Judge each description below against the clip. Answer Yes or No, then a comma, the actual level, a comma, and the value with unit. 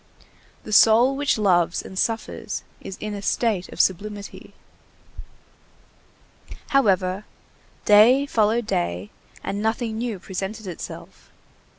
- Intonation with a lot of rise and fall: No, average, 3.1 semitones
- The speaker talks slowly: Yes, slow, 105 wpm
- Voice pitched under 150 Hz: No, high, 210 Hz